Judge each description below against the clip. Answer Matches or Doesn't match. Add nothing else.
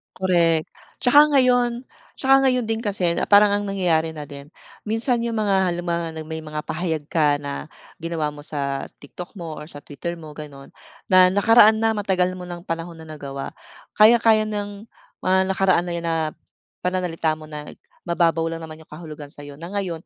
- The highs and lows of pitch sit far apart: Doesn't match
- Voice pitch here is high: Doesn't match